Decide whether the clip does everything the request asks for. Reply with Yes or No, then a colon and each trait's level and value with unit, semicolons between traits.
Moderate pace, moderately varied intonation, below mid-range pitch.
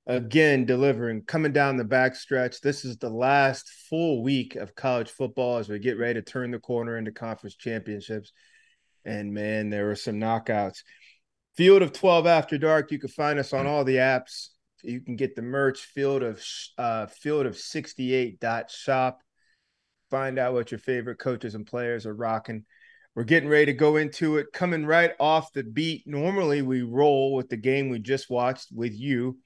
Yes: average, 185 wpm; average, 3.6 semitones; low, 130 Hz